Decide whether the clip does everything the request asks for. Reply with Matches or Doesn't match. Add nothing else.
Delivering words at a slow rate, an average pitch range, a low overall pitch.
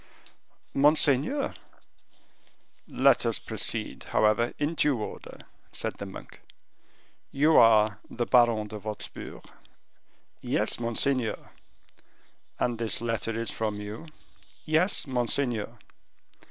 Matches